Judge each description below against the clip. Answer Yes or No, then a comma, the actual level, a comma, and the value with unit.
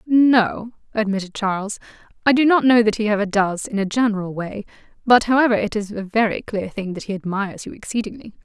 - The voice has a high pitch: Yes, high, 215 Hz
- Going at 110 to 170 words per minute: No, average, 200 wpm